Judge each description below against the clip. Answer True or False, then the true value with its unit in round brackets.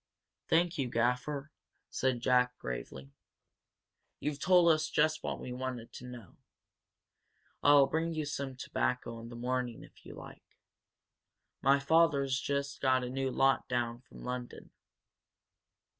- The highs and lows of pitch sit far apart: False (2.7 semitones)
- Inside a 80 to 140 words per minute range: True (135 wpm)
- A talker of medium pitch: False (130 Hz)